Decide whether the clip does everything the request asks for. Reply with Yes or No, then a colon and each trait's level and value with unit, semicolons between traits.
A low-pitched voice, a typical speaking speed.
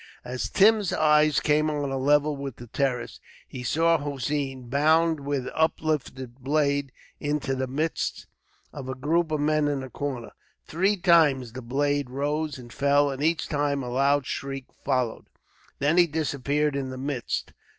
No: medium, 145 Hz; average, 160 wpm